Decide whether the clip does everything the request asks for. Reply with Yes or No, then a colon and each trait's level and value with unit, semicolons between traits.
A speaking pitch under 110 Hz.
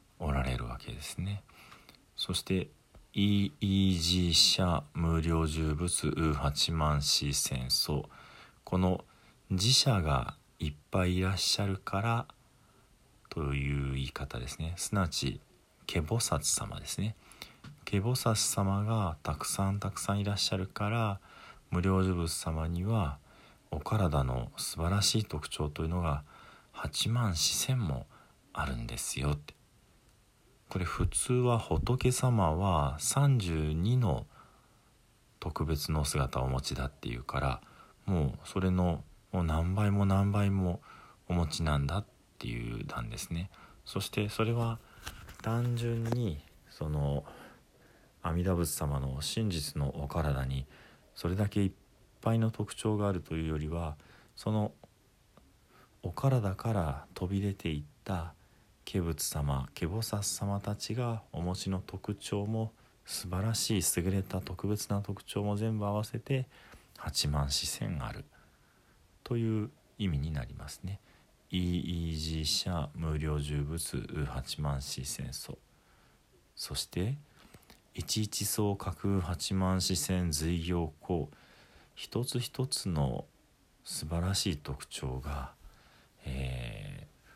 Yes: very low, 90 Hz